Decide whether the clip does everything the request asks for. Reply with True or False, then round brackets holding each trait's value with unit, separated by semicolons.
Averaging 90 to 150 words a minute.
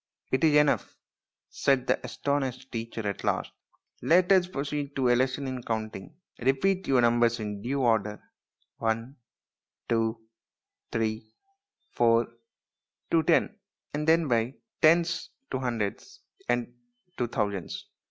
True (135 wpm)